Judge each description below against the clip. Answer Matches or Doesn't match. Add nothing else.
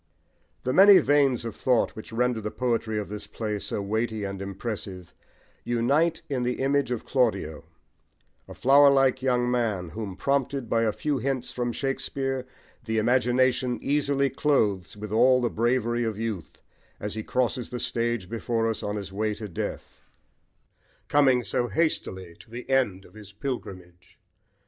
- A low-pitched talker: Matches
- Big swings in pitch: Doesn't match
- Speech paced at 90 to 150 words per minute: Doesn't match